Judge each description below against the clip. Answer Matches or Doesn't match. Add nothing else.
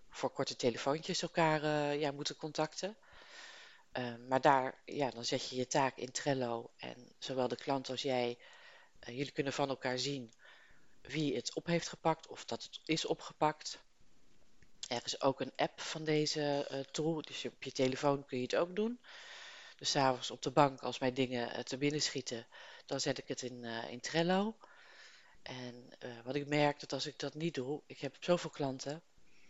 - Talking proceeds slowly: Doesn't match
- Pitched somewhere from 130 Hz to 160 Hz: Matches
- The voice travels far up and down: Doesn't match